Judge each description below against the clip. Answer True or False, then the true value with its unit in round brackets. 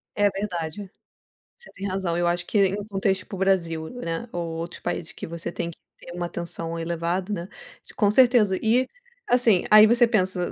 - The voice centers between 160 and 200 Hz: True (190 Hz)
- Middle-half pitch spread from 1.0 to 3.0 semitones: False (3.6 semitones)